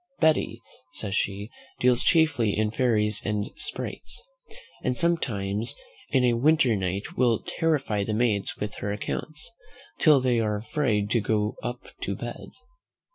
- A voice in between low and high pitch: No, low, 115 Hz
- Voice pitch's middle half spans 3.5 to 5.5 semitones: Yes, average, 4.0 semitones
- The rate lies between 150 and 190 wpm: No, average, 140 wpm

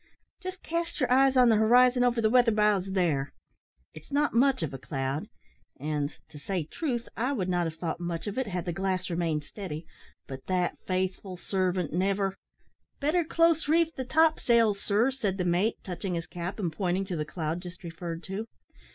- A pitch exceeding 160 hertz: Yes, high, 190 Hz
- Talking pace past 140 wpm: Yes, average, 195 wpm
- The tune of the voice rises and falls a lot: Yes, wide, 6.2 semitones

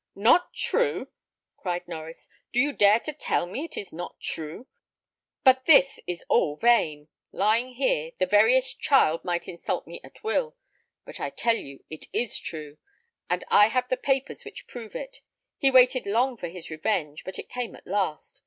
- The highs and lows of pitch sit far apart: Yes, wide, 7.1 semitones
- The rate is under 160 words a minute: No, average, 175 wpm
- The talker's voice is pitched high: Yes, high, 215 Hz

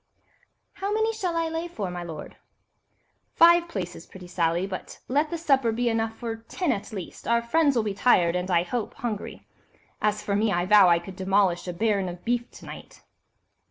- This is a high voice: Yes, high, 215 Hz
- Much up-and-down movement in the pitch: Yes, wide, 6.6 semitones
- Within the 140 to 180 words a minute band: No, average, 195 wpm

